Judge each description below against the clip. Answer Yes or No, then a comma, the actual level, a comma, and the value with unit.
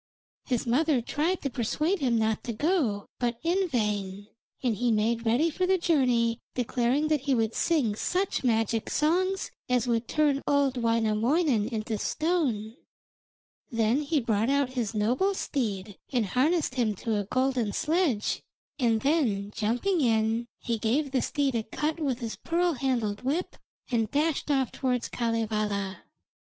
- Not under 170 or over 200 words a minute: No, average, 155 wpm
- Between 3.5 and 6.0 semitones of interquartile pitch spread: Yes, average, 5.1 semitones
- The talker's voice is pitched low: No, high, 245 Hz